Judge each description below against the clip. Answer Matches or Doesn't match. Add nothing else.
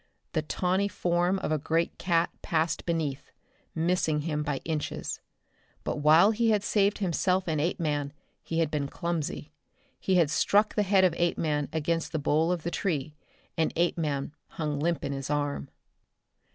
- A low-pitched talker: Doesn't match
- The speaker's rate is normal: Matches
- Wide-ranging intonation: Doesn't match